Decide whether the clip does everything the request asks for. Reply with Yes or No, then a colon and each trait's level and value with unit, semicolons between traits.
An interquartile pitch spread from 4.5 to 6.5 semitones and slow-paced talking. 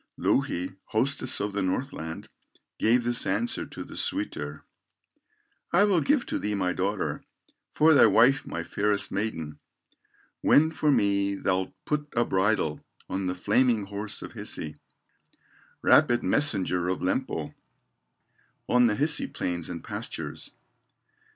Yes: wide, 5.5 semitones; slow, 130 wpm